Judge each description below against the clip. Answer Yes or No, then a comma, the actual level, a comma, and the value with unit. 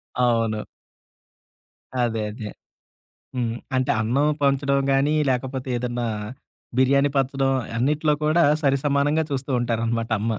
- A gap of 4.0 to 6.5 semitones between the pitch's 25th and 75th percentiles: No, average, 2.9 semitones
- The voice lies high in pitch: No, low, 130 Hz